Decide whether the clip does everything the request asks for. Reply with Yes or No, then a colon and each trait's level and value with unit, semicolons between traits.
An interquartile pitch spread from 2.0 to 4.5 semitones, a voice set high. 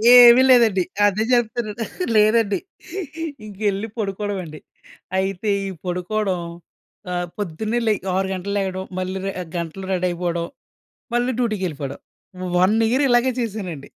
Yes: average, 3.2 semitones; high, 195 Hz